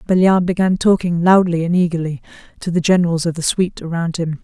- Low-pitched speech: No, medium, 175 Hz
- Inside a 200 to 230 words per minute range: No, average, 190 wpm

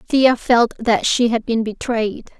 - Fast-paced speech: No, average, 175 wpm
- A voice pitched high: Yes, high, 230 Hz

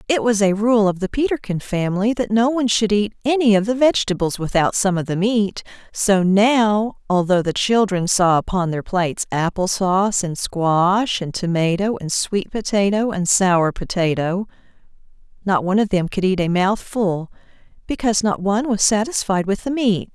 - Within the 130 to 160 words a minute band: No, average, 175 wpm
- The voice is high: Yes, high, 200 Hz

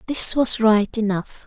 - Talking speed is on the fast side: No, average, 165 wpm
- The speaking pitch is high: Yes, high, 220 Hz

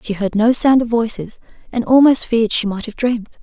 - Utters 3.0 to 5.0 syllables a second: No, 5.6 syllables/s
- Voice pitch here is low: No, high, 230 Hz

